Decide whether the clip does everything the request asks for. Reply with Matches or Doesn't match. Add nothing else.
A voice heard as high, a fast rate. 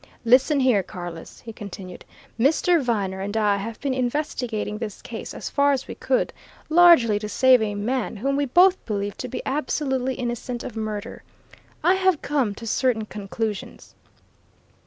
Doesn't match